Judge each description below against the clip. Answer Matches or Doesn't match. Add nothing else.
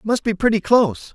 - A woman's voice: Doesn't match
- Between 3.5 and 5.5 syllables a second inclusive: Doesn't match